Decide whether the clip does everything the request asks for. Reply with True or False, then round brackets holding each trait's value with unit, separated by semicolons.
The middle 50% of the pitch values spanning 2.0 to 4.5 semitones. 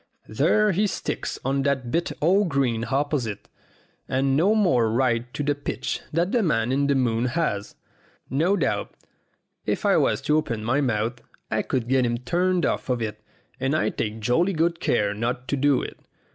False (5.3 semitones)